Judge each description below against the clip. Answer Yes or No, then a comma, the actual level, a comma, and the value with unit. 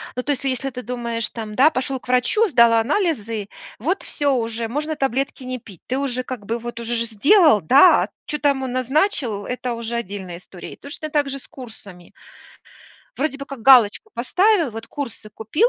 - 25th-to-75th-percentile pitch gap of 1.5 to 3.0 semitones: No, average, 3.7 semitones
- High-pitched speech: Yes, very high, 250 Hz